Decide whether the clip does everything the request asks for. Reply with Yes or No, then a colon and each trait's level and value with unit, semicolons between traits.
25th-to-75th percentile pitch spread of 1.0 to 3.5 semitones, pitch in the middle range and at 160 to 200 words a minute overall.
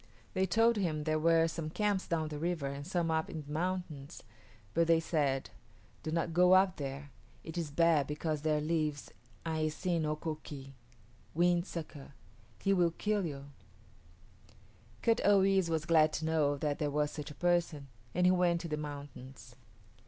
Yes: average, 2.8 semitones; medium, 160 Hz; average, 180 wpm